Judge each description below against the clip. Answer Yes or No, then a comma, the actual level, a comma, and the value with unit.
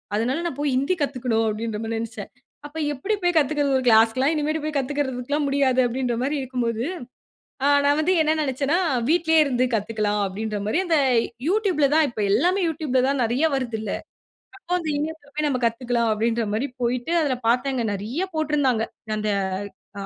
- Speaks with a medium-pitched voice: No, very high, 265 Hz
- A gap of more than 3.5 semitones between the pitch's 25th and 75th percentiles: Yes, average, 4.6 semitones